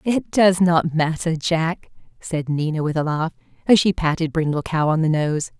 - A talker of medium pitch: Yes, medium, 165 Hz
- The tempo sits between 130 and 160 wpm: No, average, 195 wpm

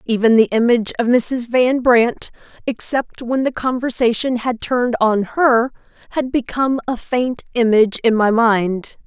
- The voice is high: Yes, high, 240 Hz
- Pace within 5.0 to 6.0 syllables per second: No, 4.5 syllables/s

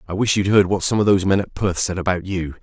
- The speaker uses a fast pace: Yes, fast, 320 wpm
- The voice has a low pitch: Yes, very low, 95 Hz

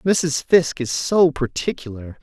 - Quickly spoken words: No, slow, 135 wpm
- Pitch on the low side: No, medium, 145 Hz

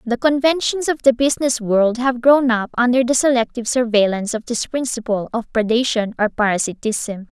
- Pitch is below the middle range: No, high, 240 Hz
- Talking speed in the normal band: Yes, average, 160 wpm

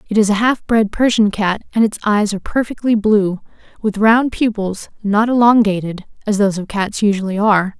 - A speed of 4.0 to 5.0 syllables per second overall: No, 5.4 syllables/s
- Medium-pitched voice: No, high, 210 Hz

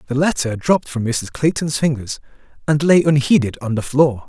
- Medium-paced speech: Yes, average, 180 wpm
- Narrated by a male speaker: Yes, male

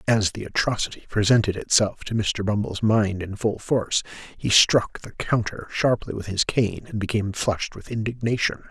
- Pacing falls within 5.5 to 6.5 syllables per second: No, 5.1 syllables/s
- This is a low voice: Yes, low, 105 Hz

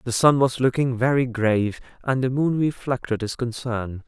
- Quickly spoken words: No, average, 175 wpm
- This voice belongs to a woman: No, male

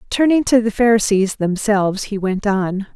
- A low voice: No, high, 210 Hz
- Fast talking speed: No, average, 165 wpm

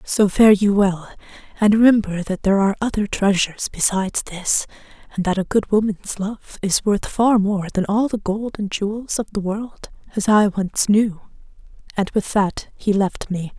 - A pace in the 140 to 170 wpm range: No, average, 180 wpm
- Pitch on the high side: Yes, high, 200 Hz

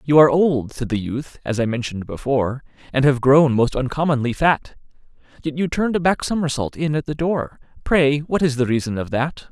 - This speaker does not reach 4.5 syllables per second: No, 5.5 syllables/s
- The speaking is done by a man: Yes, male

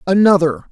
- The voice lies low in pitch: No, high, 190 Hz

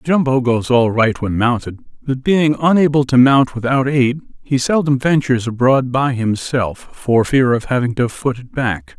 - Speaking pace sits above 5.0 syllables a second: No, 4.5 syllables/s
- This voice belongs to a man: Yes, male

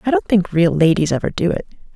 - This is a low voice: No, medium, 175 Hz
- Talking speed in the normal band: No, fast, 245 wpm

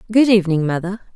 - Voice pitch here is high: Yes, high, 195 Hz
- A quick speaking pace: No, average, 155 wpm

